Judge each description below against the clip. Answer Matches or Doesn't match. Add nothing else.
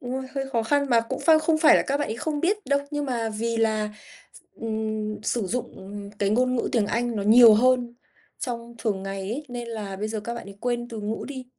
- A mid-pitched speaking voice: Doesn't match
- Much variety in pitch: Doesn't match